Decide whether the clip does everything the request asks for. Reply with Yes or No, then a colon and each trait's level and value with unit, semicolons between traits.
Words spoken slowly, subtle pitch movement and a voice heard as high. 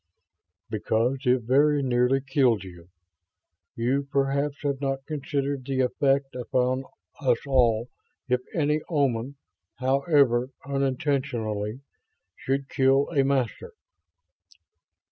No: slow, 100 wpm; narrow, 2.0 semitones; low, 135 Hz